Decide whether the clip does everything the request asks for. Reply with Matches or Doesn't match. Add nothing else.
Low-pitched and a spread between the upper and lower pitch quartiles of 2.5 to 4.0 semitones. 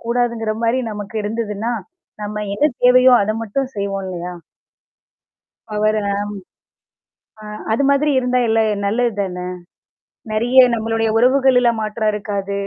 Doesn't match